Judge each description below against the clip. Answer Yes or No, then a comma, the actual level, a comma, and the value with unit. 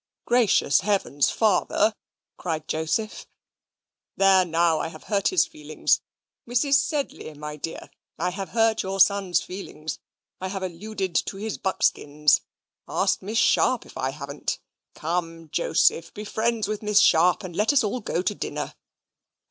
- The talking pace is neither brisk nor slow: Yes, average, 150 wpm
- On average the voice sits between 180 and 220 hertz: Yes, high, 190 Hz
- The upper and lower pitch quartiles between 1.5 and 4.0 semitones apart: No, average, 4.5 semitones